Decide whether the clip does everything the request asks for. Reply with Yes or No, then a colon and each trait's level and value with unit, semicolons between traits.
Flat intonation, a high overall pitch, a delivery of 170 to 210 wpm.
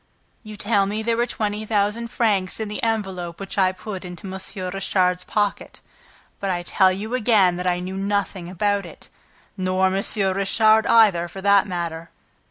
Yes: narrow, 2.3 semitones; high, 195 Hz; average, 175 wpm